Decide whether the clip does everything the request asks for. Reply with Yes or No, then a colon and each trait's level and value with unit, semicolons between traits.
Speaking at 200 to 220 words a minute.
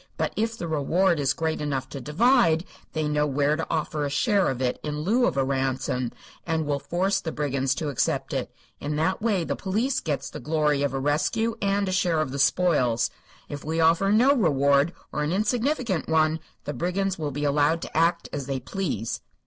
Yes: fast, 205 wpm